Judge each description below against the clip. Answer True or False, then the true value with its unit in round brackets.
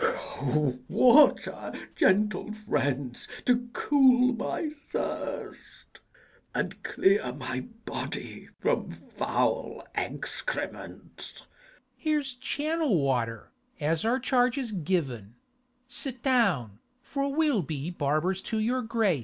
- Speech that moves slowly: True (105 wpm)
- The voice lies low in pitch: False (215 Hz)